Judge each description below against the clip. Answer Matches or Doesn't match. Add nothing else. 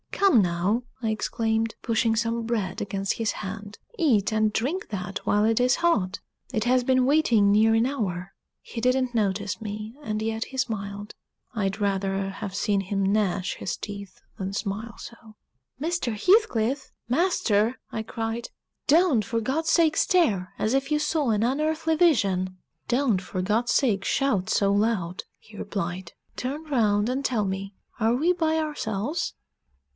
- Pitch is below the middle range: Doesn't match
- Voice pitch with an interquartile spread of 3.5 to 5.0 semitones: Matches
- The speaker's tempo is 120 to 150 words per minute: Doesn't match